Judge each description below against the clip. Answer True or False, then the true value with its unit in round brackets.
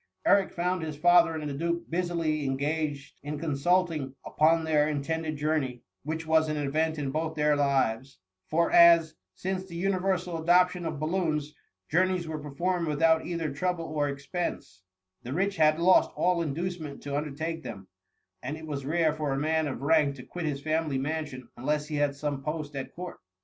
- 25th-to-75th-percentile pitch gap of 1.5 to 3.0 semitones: True (2.7 semitones)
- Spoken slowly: False (180 wpm)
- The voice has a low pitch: False (155 Hz)